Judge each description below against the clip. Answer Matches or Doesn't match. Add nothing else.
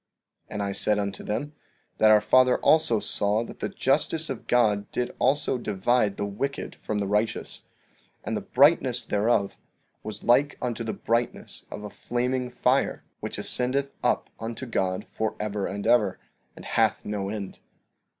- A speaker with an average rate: Matches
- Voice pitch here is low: Matches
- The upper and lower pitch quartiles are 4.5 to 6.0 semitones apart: Doesn't match